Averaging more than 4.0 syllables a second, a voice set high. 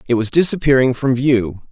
No: 5.0 syllables/s; low, 130 Hz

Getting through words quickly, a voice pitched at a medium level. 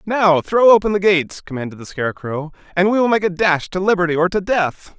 Yes: fast, 230 wpm; medium, 180 Hz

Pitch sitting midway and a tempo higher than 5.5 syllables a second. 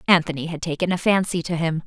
Yes: medium, 170 Hz; 6.5 syllables/s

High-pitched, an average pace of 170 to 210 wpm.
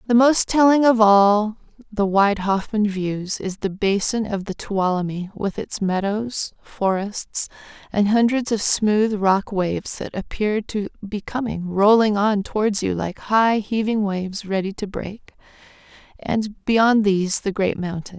No: high, 205 Hz; average, 155 wpm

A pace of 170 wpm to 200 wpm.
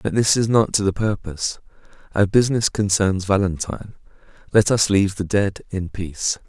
No: average, 155 wpm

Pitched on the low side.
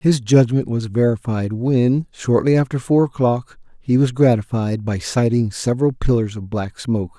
Yes: low, 120 Hz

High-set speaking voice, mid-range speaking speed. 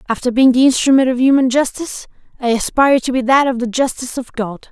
No: very high, 255 Hz; fast, 215 wpm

